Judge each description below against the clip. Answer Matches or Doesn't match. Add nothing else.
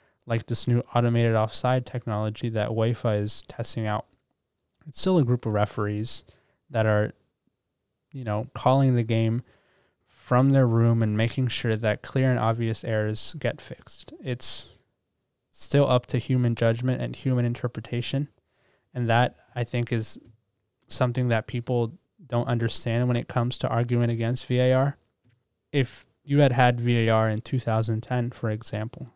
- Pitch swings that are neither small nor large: Doesn't match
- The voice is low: Matches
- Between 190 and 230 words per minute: Doesn't match